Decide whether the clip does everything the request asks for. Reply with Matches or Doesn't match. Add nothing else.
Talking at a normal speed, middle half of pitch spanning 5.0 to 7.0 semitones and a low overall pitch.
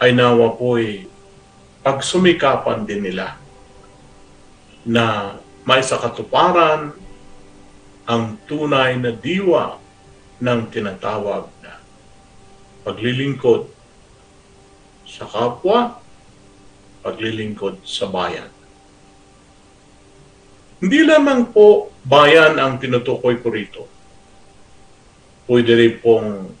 Doesn't match